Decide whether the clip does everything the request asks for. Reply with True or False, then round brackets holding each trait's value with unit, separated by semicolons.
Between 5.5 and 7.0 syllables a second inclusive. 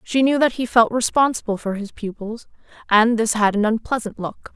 False (5.2 syllables/s)